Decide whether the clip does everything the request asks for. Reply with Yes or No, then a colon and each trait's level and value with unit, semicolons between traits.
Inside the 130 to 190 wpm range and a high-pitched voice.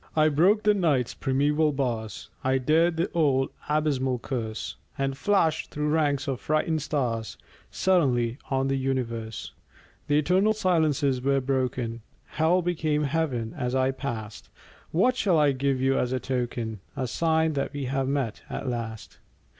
No: average, 155 wpm; low, 135 Hz